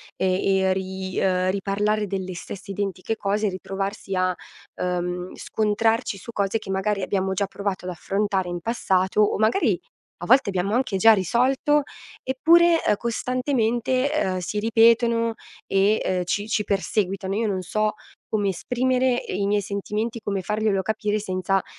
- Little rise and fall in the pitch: No, average, 3.0 semitones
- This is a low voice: No, high, 205 Hz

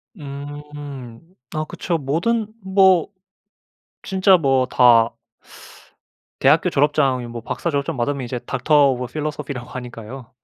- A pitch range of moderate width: Yes, average, 3.6 semitones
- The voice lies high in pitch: No, medium, 140 Hz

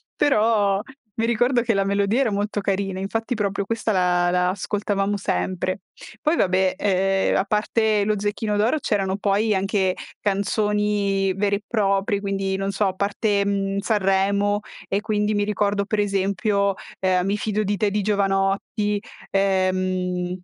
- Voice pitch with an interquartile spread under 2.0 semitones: Yes, narrow, 1.3 semitones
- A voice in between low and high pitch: No, high, 200 Hz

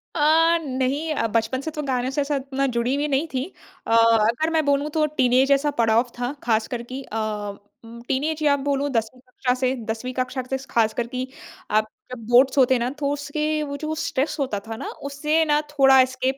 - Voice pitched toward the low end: No, very high, 265 Hz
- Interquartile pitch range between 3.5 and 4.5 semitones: No, average, 3.0 semitones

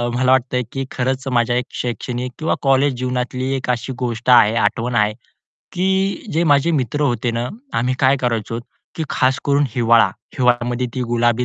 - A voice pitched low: Yes, low, 125 Hz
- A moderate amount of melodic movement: No, narrow, 2.1 semitones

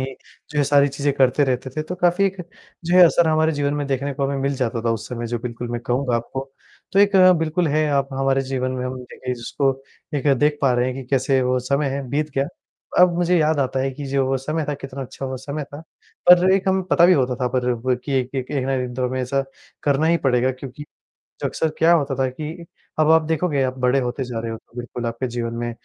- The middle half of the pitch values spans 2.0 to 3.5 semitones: Yes, average, 3.1 semitones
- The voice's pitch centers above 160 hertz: No, low, 135 Hz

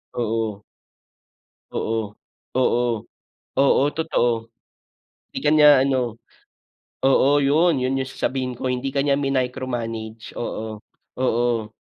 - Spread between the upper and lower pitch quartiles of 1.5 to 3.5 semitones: Yes, average, 3.2 semitones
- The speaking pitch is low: Yes, low, 125 Hz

